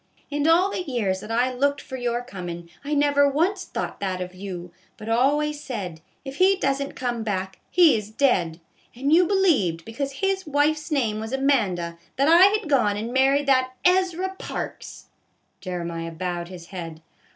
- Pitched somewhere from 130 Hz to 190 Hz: No, very high, 255 Hz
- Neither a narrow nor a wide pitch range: No, wide, 7.8 semitones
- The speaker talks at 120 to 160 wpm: No, average, 180 wpm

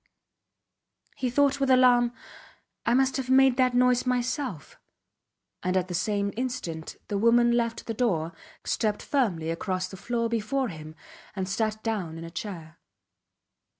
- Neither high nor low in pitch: No, high, 230 Hz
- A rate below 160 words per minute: Yes, average, 150 wpm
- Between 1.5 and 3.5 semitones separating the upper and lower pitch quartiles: No, wide, 5.4 semitones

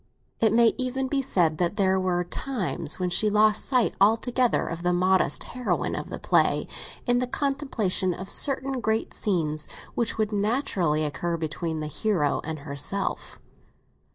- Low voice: No, high, 200 Hz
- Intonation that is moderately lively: No, wide, 6.0 semitones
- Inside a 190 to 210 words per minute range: No, average, 155 wpm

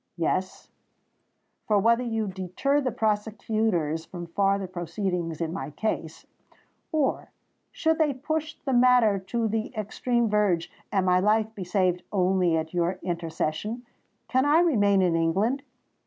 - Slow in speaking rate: Yes, slow, 130 wpm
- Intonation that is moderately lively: Yes, average, 4.7 semitones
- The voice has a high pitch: Yes, high, 205 Hz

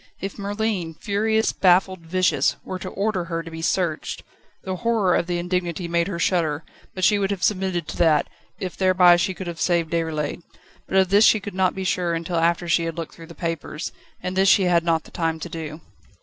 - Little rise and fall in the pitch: Yes, narrow, 2.2 semitones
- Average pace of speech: No, fast, 220 wpm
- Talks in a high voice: No, medium, 175 Hz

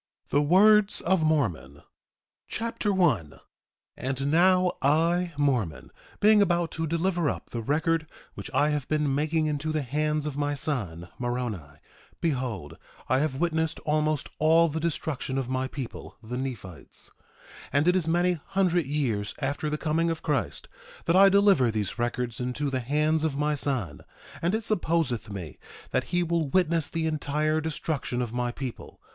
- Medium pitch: Yes, medium, 150 Hz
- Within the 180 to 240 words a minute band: No, average, 160 wpm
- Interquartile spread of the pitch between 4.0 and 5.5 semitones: Yes, average, 4.5 semitones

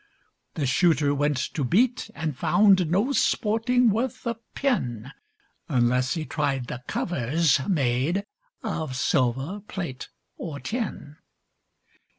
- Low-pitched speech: No, medium, 160 Hz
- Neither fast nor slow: No, slow, 115 wpm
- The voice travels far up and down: Yes, wide, 7.7 semitones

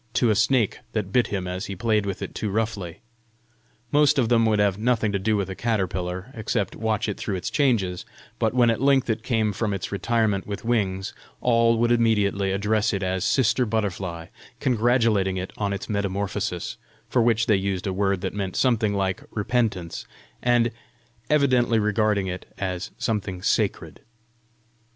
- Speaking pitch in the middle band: No, low, 105 Hz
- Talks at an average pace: Yes, average, 175 wpm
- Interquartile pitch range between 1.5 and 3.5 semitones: Yes, average, 3.2 semitones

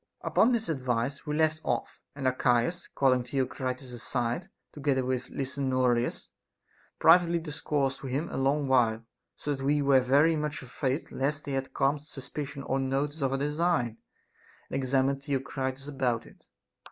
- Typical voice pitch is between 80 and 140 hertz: Yes, low, 135 Hz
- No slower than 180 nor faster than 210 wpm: No, average, 150 wpm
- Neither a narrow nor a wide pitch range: No, narrow, 2.3 semitones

